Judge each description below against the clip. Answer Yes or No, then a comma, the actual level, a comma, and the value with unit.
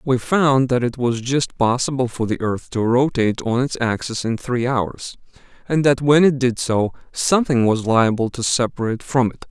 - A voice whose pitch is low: Yes, low, 125 Hz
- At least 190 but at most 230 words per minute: Yes, average, 195 wpm